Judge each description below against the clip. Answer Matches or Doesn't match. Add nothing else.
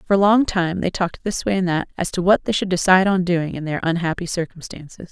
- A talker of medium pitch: Matches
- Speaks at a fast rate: Matches